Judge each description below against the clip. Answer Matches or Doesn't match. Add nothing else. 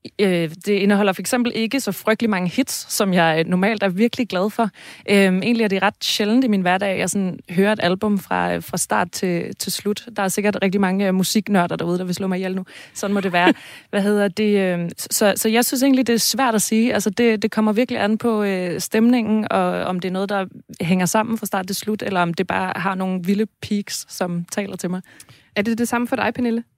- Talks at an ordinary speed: Doesn't match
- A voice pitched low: Doesn't match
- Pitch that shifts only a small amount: Doesn't match